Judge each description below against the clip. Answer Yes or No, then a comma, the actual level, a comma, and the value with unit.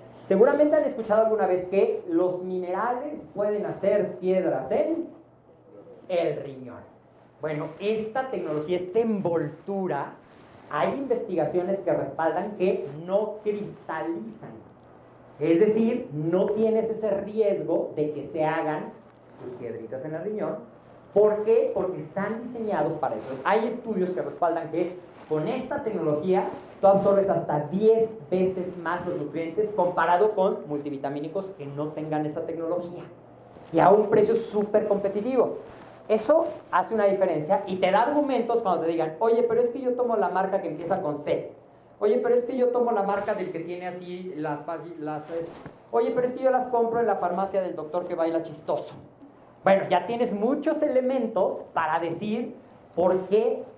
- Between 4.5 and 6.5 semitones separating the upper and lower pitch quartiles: Yes, average, 5.2 semitones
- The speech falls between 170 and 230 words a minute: No, average, 155 wpm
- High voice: Yes, high, 195 Hz